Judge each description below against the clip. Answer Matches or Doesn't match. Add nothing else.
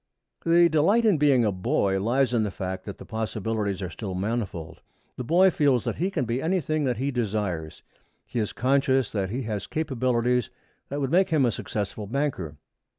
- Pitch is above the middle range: Doesn't match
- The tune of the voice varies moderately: Doesn't match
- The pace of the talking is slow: Doesn't match